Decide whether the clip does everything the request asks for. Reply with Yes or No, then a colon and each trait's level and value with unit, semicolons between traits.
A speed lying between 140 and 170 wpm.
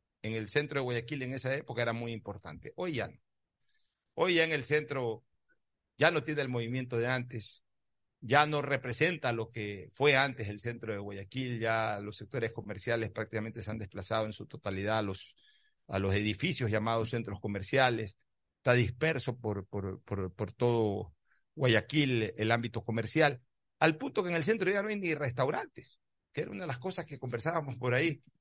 No: average, 185 wpm